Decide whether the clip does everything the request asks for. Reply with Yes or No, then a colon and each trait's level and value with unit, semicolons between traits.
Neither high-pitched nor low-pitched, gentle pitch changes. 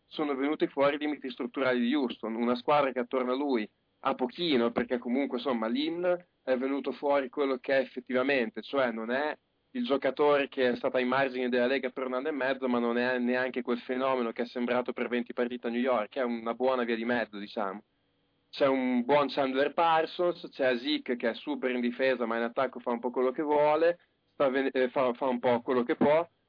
No: low, 130 Hz; narrow, 2.2 semitones